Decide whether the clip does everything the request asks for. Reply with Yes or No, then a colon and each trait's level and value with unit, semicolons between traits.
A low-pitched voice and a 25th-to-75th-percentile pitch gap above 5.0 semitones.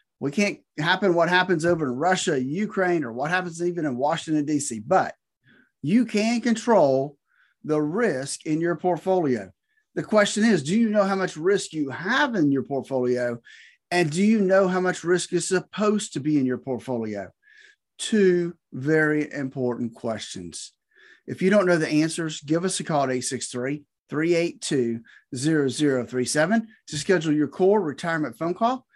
No: medium, 165 Hz; wide, 5.4 semitones